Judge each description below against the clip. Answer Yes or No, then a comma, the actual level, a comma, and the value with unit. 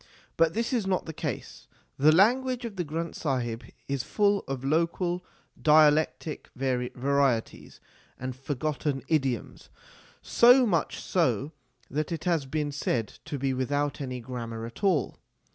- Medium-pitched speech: Yes, medium, 150 Hz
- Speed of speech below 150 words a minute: Yes, average, 140 wpm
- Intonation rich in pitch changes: No, average, 4.7 semitones